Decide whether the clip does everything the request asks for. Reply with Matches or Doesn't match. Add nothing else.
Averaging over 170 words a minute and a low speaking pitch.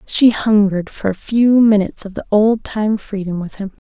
Doesn't match